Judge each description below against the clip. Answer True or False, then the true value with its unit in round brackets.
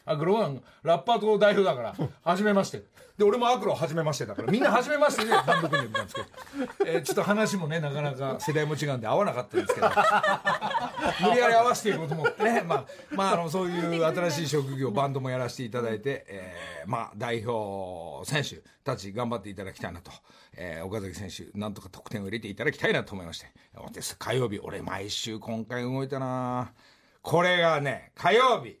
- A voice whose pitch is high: False (145 Hz)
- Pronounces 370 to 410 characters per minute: True (400 characters per minute)